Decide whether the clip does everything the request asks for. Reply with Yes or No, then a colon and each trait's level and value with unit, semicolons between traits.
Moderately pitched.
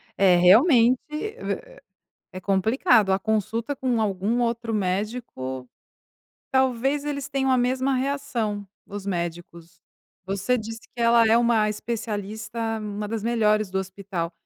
No: high, 220 Hz